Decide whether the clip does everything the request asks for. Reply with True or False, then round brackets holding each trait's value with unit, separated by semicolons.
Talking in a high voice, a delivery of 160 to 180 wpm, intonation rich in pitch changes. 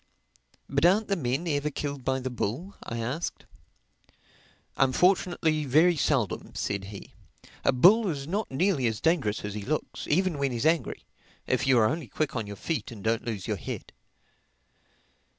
False (140 Hz; 170 wpm; 6.1 semitones)